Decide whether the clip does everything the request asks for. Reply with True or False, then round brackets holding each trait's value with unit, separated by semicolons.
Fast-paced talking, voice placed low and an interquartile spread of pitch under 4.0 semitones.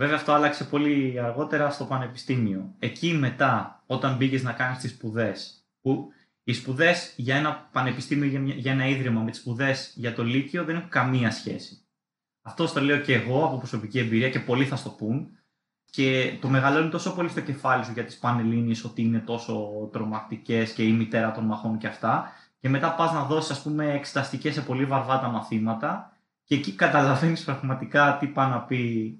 True (185 wpm; 130 Hz; 3.5 semitones)